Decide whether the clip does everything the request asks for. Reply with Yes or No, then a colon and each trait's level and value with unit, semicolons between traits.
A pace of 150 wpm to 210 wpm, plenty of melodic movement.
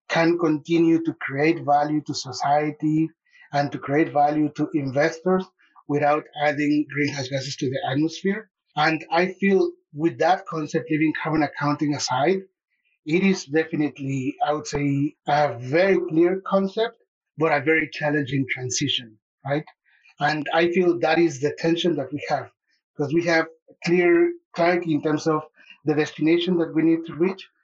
No: average, 155 wpm; narrow, 2.6 semitones